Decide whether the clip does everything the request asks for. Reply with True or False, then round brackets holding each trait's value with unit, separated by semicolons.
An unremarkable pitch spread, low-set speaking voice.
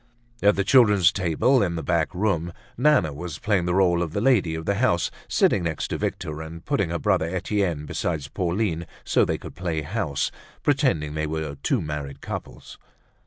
True (4.2 semitones; 85 Hz)